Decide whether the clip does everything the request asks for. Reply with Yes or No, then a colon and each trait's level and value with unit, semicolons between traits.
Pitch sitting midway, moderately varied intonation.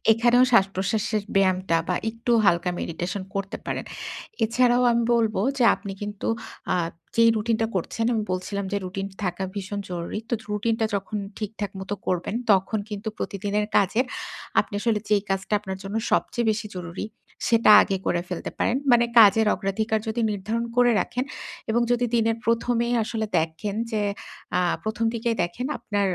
No: high, 210 Hz; average, 3.0 semitones